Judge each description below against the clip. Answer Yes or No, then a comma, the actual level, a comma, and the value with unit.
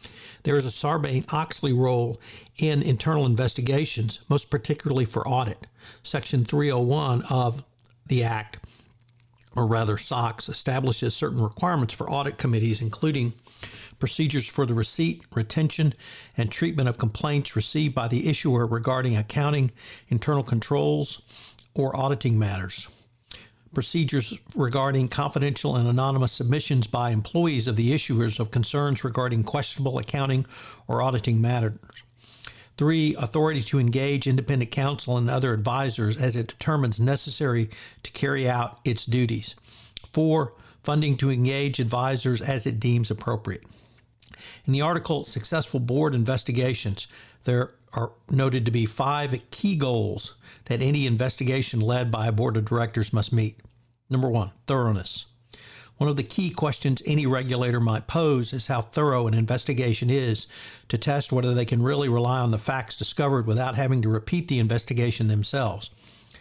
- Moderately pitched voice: No, low, 125 Hz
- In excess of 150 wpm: No, average, 140 wpm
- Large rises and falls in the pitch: No, average, 3.2 semitones